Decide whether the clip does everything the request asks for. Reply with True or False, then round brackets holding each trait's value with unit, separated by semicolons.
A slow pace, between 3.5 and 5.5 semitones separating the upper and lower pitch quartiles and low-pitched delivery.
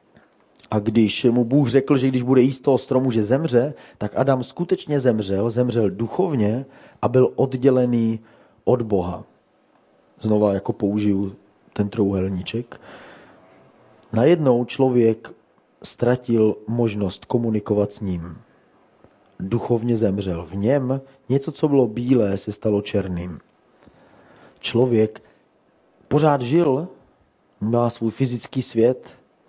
True (110 wpm; 3.8 semitones; 120 Hz)